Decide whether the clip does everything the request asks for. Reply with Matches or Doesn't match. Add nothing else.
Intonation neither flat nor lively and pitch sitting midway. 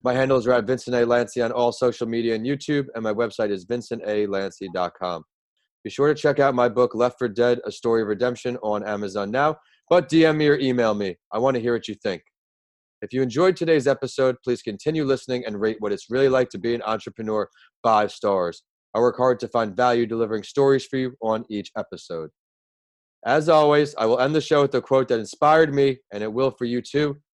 Doesn't match